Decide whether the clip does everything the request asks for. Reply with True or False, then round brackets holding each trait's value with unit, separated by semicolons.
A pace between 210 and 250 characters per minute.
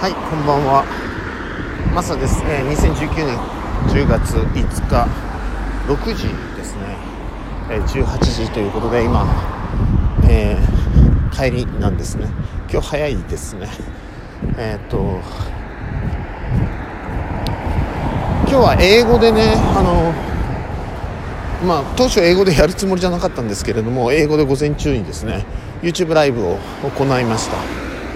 True (230 characters per minute)